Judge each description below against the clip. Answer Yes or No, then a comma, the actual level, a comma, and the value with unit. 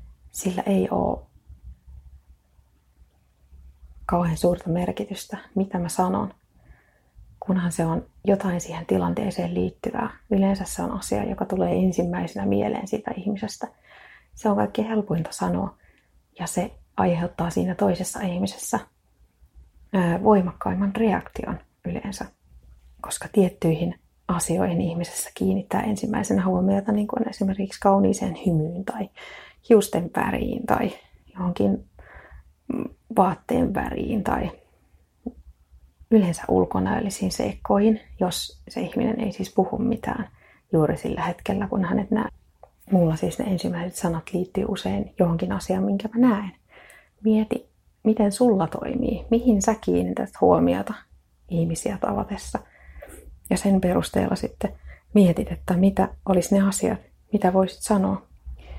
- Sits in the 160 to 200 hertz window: Yes, medium, 185 Hz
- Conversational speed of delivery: Yes, average, 115 wpm